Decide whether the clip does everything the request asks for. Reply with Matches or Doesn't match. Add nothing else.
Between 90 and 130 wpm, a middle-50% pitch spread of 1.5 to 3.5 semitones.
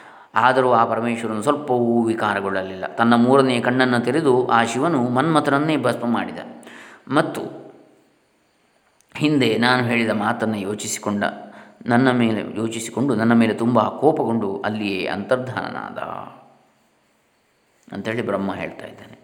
Matches